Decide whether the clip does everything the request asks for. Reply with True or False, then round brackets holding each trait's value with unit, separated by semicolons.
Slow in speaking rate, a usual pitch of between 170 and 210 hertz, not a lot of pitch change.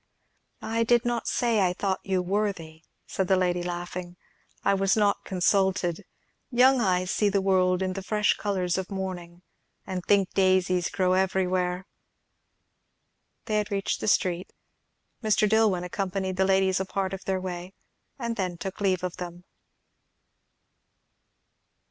False (145 wpm; 190 Hz; 1.8 semitones)